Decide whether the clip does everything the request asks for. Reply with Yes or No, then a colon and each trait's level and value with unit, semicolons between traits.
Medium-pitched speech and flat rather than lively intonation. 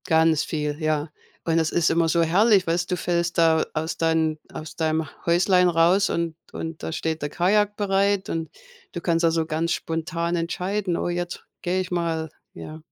Yes: medium, 165 Hz; narrow, 1.8 semitones